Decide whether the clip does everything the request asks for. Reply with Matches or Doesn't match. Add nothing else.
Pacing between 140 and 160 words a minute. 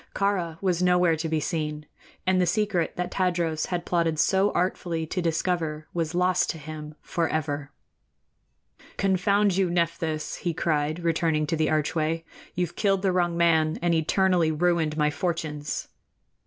Matches